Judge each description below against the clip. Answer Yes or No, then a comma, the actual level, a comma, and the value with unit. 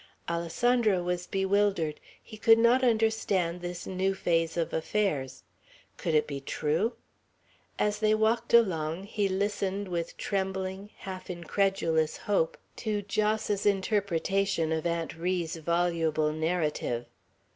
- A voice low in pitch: No, medium, 185 Hz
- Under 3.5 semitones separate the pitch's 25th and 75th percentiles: No, average, 3.8 semitones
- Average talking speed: No, slow, 120 wpm